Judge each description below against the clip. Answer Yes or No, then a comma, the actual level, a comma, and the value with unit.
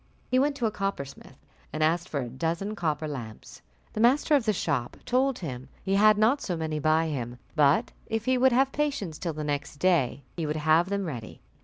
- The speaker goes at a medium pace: No, fast, 210 wpm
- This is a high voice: No, medium, 165 Hz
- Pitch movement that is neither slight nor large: No, wide, 6.7 semitones